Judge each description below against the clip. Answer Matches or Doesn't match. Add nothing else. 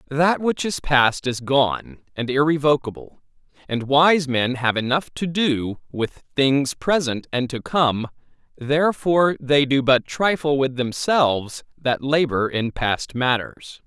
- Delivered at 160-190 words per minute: Doesn't match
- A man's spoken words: Matches